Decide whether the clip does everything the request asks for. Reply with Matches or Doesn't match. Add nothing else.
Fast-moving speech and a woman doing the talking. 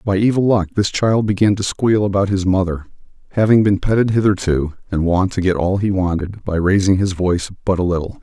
Doesn't match